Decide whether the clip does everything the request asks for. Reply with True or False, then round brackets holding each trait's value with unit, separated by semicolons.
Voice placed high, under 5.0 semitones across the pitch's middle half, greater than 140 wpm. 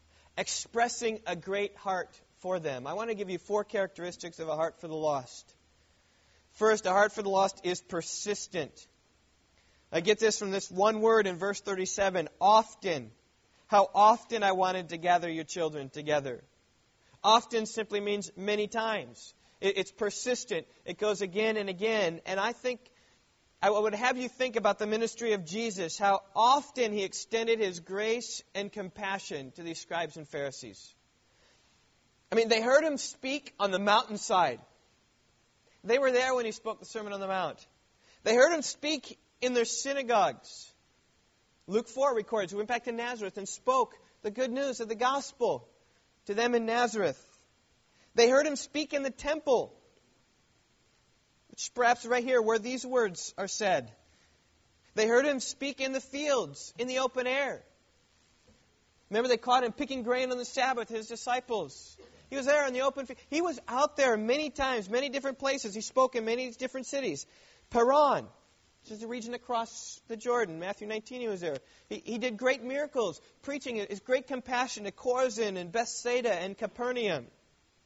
True (220 Hz; 4.5 semitones; 170 wpm)